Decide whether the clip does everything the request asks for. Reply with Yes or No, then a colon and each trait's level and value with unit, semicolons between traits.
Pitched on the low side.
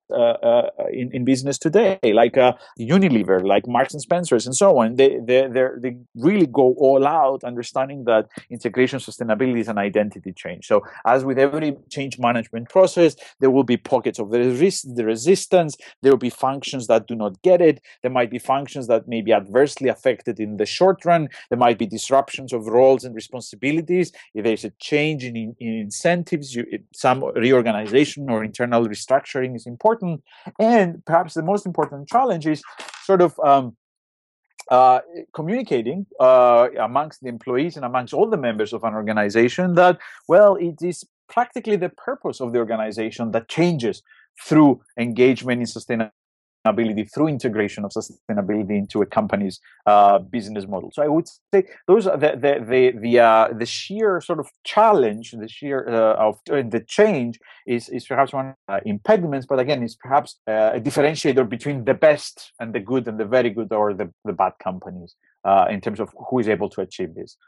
Yes: low, 130 Hz